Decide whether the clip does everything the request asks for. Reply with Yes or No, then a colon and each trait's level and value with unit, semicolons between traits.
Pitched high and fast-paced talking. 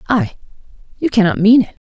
No: high, 220 Hz; slow, 130 wpm